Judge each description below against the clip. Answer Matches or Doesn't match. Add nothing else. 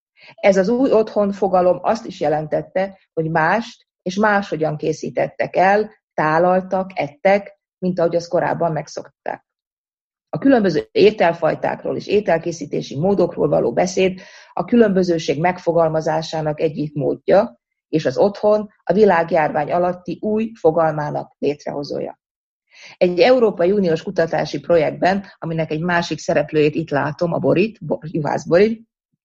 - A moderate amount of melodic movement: Matches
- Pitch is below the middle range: Doesn't match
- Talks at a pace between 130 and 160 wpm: Doesn't match